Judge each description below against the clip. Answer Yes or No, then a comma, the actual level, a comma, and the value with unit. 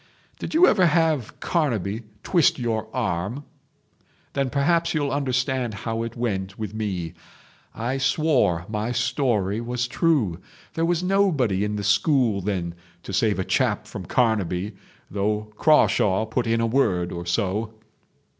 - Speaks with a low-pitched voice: Yes, low, 115 Hz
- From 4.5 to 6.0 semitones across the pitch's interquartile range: Yes, wide, 5.5 semitones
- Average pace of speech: Yes, average, 145 wpm